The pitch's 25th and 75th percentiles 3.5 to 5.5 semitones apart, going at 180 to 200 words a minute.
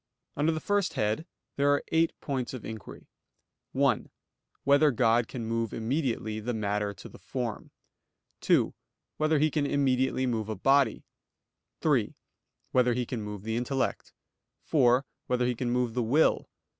No: average, 3.9 semitones; average, 155 wpm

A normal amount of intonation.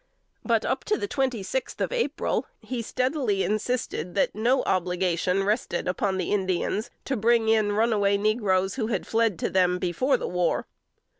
Yes: average, 4.2 semitones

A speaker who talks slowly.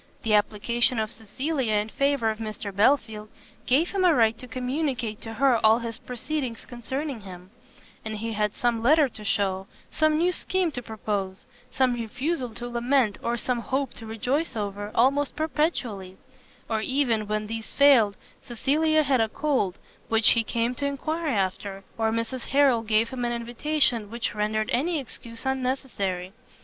No: average, 165 wpm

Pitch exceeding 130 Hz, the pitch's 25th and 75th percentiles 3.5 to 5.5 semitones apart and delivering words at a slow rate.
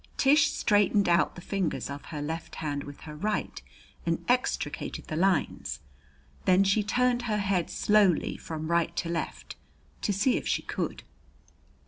No: high, 190 Hz; average, 4.6 semitones; average, 155 wpm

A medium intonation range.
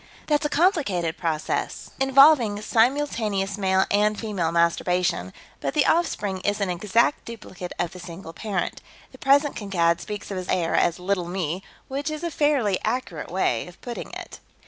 No: wide, 6.5 semitones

